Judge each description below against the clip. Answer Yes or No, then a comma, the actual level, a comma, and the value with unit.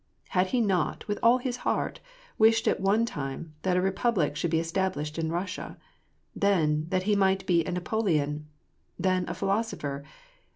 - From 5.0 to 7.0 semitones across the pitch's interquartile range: No, average, 4.2 semitones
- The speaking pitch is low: No, medium, 185 Hz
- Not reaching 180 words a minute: Yes, average, 170 wpm